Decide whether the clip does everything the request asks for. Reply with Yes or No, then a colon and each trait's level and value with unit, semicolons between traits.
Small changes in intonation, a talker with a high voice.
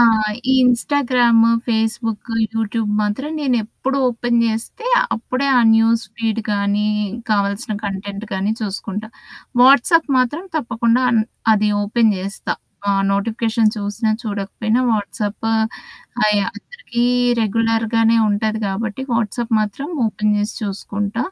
Yes: narrow, 2.3 semitones; high, 225 Hz